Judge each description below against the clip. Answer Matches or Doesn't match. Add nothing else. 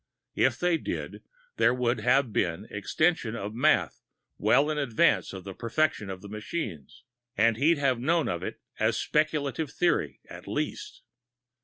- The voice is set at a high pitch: Doesn't match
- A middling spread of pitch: Doesn't match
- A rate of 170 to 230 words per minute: Doesn't match